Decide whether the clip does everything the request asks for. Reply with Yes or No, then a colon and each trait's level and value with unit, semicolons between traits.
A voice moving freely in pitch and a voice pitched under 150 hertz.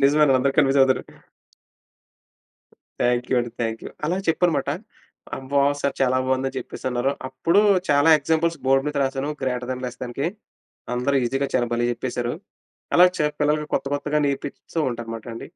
No: average, 2.8 semitones; low, 135 Hz